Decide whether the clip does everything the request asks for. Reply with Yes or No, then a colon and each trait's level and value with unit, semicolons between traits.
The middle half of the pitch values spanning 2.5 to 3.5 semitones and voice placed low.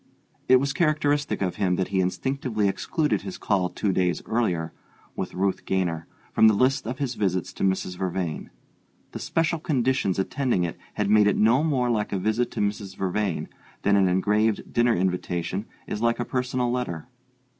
No: average, 5.2 semitones; low, 105 Hz